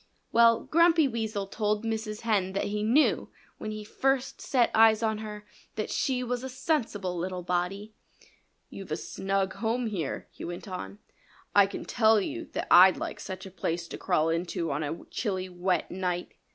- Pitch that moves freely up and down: No, average, 3.6 semitones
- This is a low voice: No, high, 210 Hz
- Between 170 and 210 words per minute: Yes, average, 180 wpm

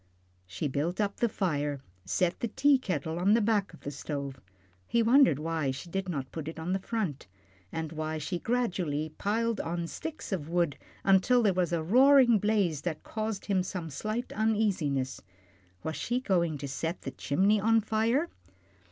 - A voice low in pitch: No, medium, 180 Hz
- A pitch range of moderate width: No, wide, 5.8 semitones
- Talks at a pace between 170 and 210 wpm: Yes, average, 175 wpm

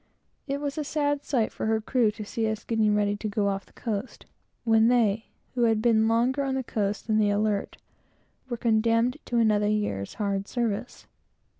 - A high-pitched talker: Yes, high, 220 Hz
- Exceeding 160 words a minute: Yes, average, 190 wpm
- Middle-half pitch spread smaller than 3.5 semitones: Yes, narrow, 2.5 semitones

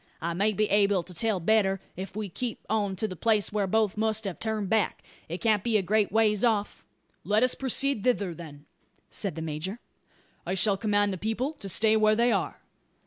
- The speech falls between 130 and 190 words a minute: No, fast, 205 wpm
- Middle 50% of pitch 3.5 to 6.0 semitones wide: No, narrow, 2.5 semitones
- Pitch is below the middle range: No, high, 210 Hz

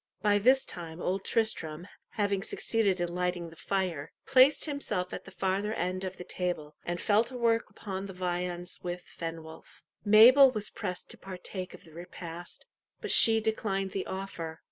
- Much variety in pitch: No, average, 3.3 semitones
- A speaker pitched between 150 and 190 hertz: Yes, medium, 185 Hz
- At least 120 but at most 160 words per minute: No, average, 170 wpm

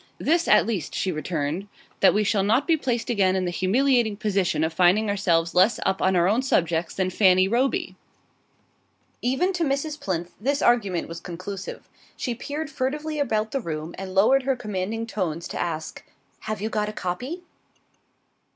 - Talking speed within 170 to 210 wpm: Yes, average, 175 wpm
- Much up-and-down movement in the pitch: Yes, wide, 5.8 semitones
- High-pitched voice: Yes, high, 205 Hz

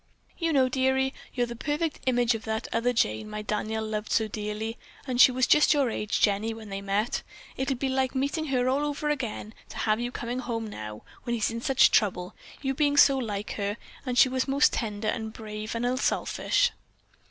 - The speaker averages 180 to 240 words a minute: Yes, fast, 205 wpm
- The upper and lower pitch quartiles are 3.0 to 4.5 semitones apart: Yes, average, 3.7 semitones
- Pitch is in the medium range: No, high, 240 Hz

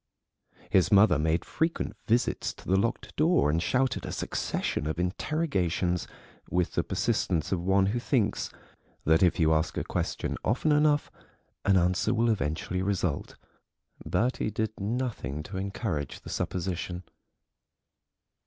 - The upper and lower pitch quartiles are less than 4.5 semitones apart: No, average, 5.1 semitones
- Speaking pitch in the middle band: No, very low, 95 Hz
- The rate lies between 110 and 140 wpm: Yes, slow, 135 wpm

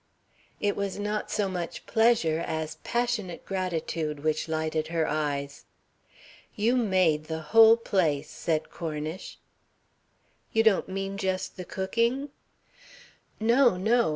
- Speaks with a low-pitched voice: No, medium, 185 Hz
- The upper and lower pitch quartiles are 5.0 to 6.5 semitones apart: Yes, wide, 5.6 semitones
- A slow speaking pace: Yes, slow, 120 wpm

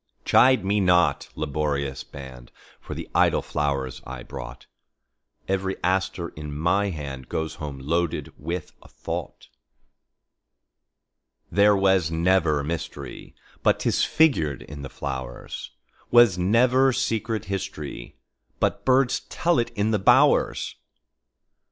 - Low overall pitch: Yes, very low, 85 Hz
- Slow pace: Yes, slow, 100 wpm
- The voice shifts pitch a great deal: Yes, wide, 6.2 semitones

